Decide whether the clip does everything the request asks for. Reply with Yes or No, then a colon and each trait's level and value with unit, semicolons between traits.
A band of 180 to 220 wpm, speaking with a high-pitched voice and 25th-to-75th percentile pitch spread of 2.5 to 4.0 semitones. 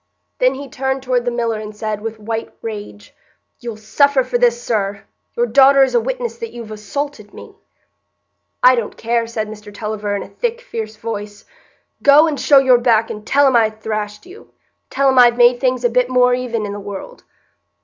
Yes: average, 200 wpm; high, 235 Hz; average, 3.5 semitones